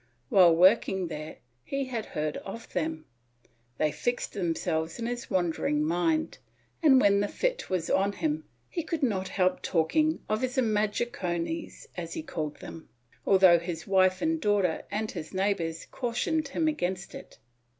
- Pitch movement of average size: No, wide, 6.7 semitones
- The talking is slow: No, average, 155 wpm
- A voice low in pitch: No, high, 195 Hz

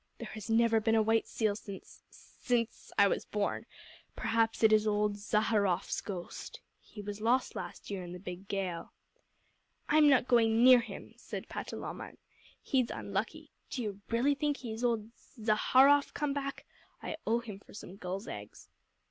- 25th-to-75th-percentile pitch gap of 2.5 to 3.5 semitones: Yes, average, 3.2 semitones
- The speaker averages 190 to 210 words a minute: No, average, 165 wpm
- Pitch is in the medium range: No, high, 220 Hz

